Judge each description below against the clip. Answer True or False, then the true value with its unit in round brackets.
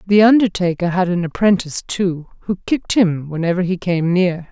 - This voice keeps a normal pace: True (175 wpm)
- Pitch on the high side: False (180 Hz)